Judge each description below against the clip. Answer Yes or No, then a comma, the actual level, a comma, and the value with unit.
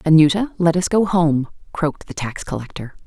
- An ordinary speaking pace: Yes, average, 175 wpm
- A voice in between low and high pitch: Yes, medium, 160 Hz